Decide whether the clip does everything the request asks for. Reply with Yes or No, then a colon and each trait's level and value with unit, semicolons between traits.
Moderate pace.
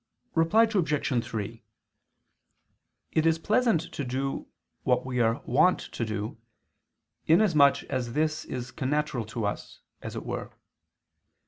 No: slow, 125 wpm